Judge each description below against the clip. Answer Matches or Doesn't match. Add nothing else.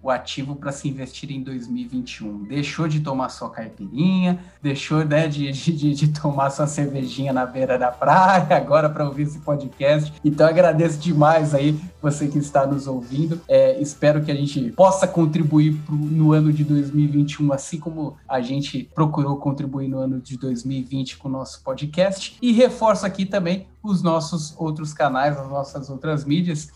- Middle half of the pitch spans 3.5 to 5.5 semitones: Doesn't match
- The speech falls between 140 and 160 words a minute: Doesn't match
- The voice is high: Doesn't match